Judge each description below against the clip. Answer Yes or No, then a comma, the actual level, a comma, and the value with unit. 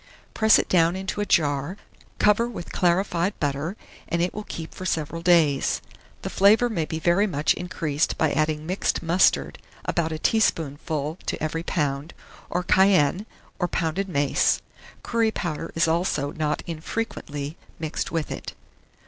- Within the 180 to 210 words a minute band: No, average, 150 wpm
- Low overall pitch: No, medium, 165 Hz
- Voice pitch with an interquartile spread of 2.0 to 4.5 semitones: Yes, average, 3.7 semitones